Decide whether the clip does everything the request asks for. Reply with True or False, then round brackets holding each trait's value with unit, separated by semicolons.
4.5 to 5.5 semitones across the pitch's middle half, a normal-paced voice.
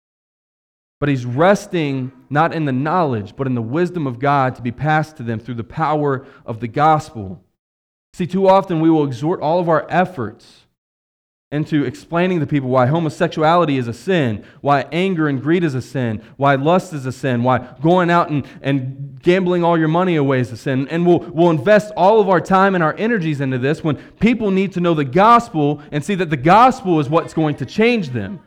False (4.9 semitones; 210 wpm)